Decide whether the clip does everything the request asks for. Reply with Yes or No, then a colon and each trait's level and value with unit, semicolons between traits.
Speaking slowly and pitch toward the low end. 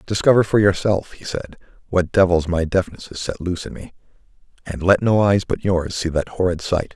No: fast, 205 wpm; very low, 90 Hz